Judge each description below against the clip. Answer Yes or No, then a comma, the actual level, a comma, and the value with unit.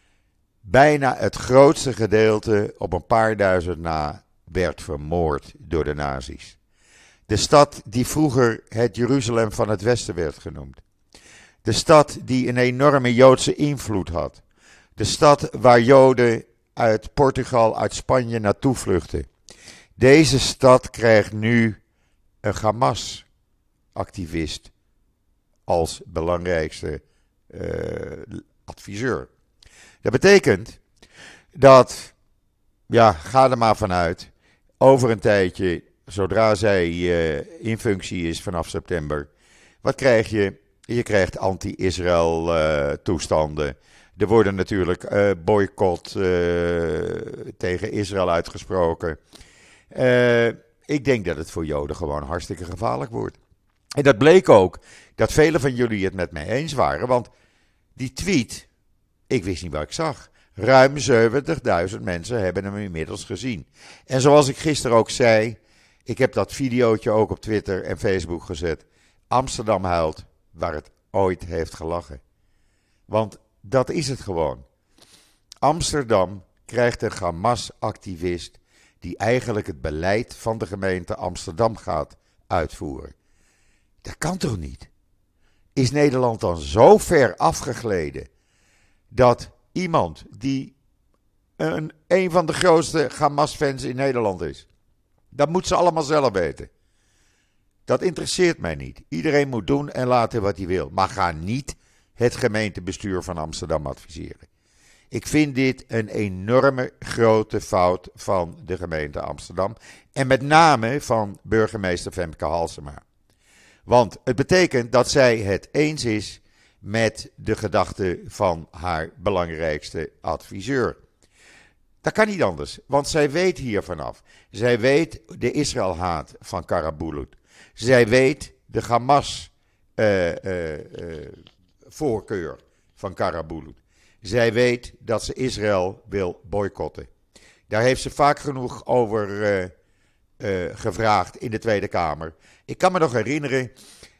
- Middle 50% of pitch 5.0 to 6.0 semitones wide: Yes, wide, 5.6 semitones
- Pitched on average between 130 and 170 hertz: No, low, 105 Hz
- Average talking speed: No, slow, 125 wpm